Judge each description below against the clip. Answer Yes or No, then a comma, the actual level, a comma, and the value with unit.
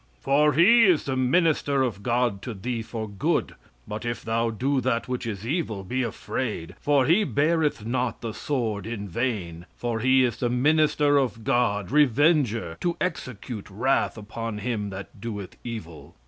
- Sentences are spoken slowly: No, average, 165 wpm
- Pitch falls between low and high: No, low, 120 Hz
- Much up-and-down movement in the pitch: No, average, 4.6 semitones